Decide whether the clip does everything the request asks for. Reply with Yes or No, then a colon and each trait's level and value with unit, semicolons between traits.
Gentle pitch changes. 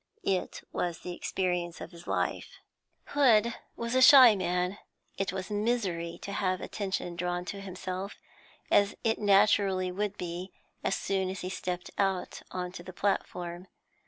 Yes: narrow, 2.2 semitones